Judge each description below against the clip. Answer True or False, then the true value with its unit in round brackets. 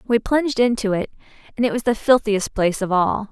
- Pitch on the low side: False (220 Hz)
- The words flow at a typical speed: False (215 wpm)